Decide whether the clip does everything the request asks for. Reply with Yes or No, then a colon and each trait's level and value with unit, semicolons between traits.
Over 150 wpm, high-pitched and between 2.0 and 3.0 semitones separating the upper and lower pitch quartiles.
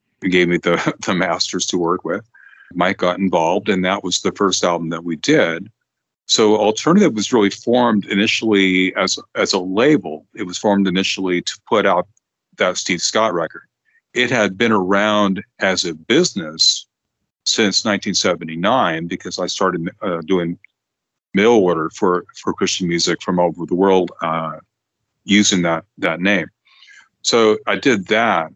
No: average, 160 wpm; very low, 95 Hz; narrow, 2.5 semitones